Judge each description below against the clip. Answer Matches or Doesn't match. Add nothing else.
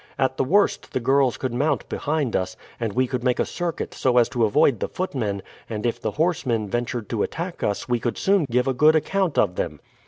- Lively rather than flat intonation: Doesn't match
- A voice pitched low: Matches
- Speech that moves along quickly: Matches